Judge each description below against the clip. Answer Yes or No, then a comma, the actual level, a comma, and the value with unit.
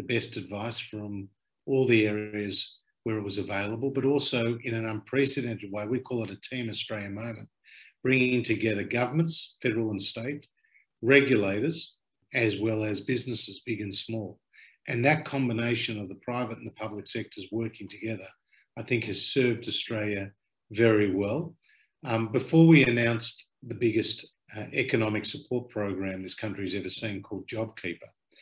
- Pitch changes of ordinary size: Yes, average, 3.0 semitones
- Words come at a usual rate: Yes, average, 150 wpm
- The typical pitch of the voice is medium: No, low, 115 Hz